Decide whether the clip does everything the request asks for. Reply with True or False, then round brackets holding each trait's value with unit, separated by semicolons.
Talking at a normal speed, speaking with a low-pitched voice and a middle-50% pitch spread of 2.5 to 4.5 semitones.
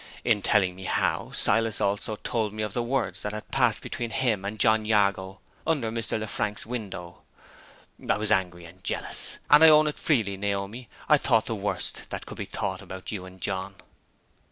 True (190 wpm; 105 Hz; 3.0 semitones)